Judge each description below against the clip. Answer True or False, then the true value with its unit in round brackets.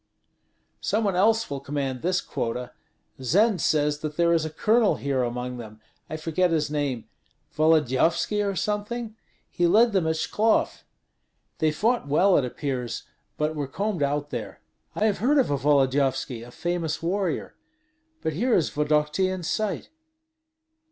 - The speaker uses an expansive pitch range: True (5.9 semitones)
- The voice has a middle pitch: True (155 Hz)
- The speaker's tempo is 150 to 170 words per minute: True (155 wpm)